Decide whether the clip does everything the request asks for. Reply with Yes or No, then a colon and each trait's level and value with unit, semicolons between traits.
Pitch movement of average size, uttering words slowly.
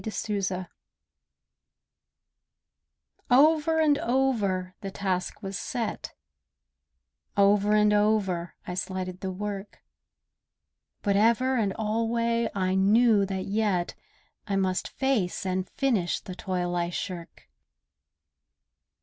Yes: average, 3.5 semitones; slow, 105 wpm